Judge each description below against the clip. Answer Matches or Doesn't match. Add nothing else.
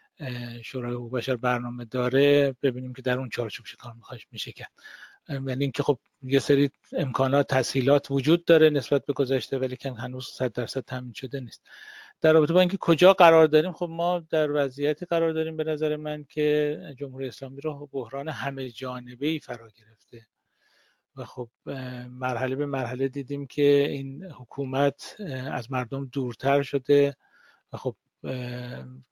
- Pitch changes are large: Doesn't match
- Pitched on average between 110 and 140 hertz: Matches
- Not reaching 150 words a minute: Doesn't match